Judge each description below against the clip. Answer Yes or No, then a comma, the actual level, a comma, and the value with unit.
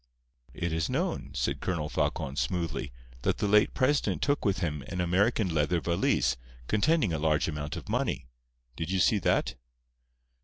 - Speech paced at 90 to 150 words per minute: No, average, 160 wpm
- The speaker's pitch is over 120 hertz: No, very low, 85 Hz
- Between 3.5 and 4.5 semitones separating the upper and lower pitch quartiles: No, average, 4.9 semitones